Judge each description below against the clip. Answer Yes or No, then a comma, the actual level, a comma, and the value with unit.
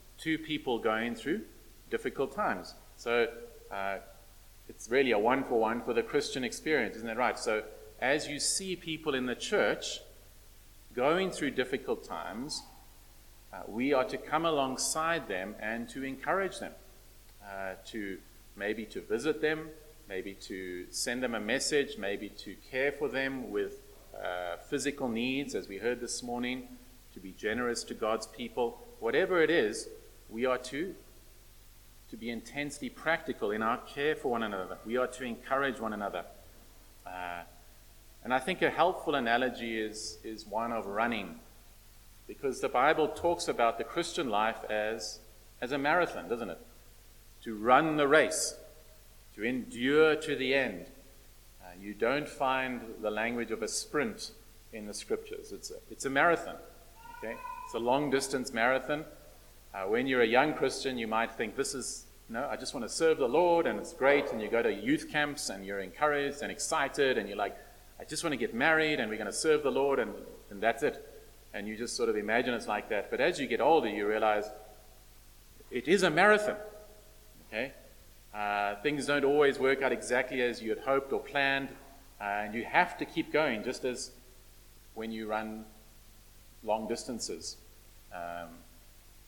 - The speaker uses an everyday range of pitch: No, wide, 6.3 semitones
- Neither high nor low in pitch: No, low, 125 Hz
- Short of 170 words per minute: No, average, 175 wpm